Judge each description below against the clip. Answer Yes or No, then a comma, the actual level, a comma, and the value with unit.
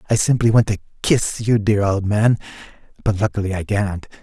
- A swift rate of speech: No, average, 185 wpm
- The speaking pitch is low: Yes, low, 105 Hz